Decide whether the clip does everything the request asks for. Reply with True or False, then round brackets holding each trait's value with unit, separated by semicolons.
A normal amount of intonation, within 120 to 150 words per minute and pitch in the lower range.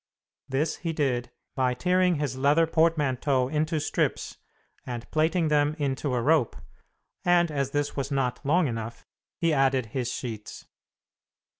False (3.7 semitones; 140 wpm; 145 Hz)